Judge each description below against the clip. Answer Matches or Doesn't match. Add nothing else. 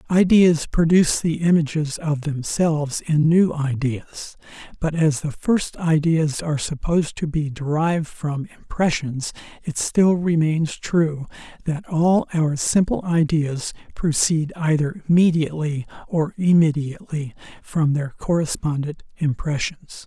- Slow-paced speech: Matches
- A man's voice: Matches